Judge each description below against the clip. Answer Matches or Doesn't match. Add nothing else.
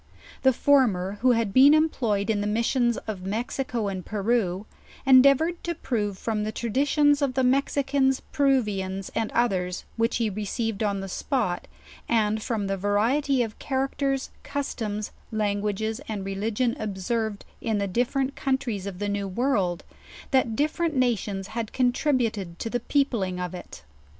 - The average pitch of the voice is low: Doesn't match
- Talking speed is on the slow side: Doesn't match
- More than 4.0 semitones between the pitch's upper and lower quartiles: Matches